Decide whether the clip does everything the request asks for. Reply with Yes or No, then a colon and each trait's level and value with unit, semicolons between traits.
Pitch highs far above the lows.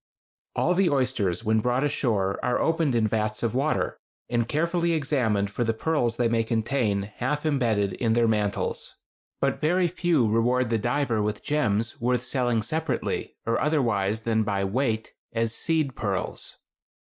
No: average, 4.5 semitones